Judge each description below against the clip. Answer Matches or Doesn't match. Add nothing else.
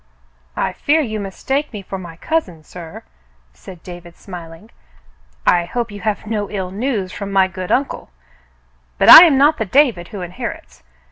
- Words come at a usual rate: Matches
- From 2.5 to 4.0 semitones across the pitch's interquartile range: Doesn't match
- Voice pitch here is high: Matches